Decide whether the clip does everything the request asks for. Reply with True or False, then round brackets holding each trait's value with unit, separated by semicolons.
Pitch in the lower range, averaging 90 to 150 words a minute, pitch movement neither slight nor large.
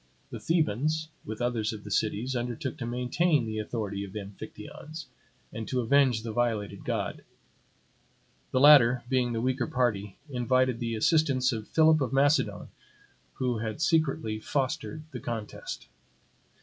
True (120 Hz; 145 wpm; 3.7 semitones)